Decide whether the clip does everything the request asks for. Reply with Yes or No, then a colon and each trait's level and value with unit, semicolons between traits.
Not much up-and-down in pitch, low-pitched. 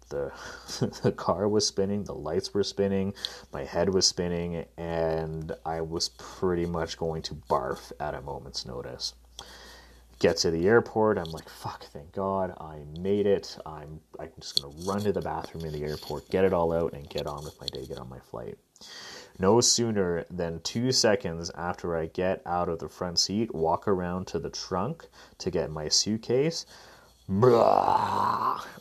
No: average, 3.9 semitones; very low, 85 Hz